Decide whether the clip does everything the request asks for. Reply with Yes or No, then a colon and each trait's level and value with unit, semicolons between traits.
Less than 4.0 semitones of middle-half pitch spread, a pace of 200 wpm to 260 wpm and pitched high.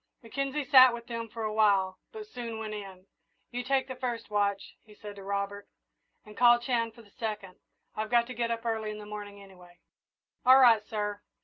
Yes: average, 2.8 semitones; fast, 205 wpm; high, 220 Hz